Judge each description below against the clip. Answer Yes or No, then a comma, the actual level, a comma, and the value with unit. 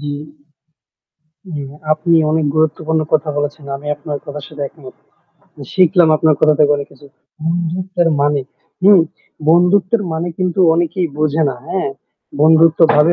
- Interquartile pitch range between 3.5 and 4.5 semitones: No, average, 2.7 semitones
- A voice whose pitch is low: No, medium, 160 Hz